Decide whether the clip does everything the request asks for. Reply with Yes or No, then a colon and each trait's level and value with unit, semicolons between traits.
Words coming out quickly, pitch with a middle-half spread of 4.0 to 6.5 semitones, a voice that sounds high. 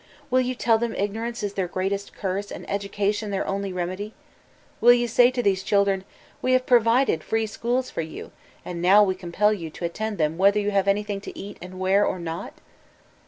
No: fast, 210 wpm; average, 3.0 semitones; high, 200 Hz